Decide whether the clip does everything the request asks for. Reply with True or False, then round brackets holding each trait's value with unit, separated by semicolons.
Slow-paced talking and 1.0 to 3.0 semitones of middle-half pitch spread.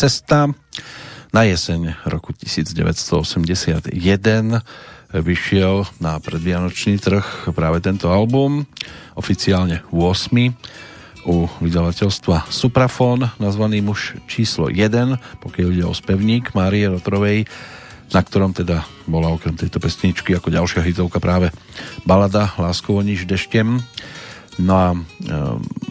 False (105 wpm; 4.0 semitones)